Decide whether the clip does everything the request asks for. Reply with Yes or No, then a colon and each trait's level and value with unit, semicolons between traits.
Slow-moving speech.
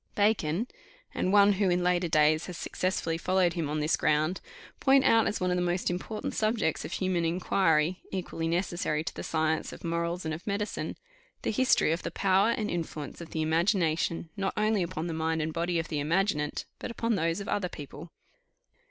No: average, 195 wpm